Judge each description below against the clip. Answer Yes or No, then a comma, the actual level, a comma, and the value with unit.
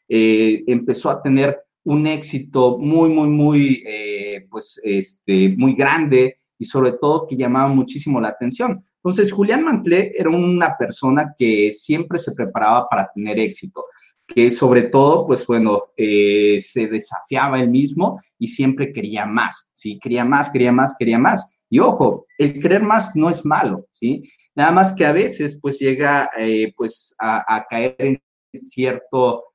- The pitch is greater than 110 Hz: Yes, low, 135 Hz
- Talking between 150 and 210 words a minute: Yes, average, 160 wpm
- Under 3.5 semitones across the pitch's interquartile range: No, average, 4.5 semitones